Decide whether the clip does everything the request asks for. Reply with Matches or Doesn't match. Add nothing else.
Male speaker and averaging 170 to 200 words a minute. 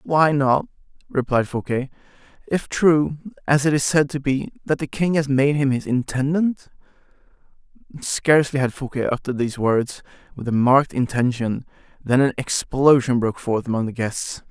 Doesn't match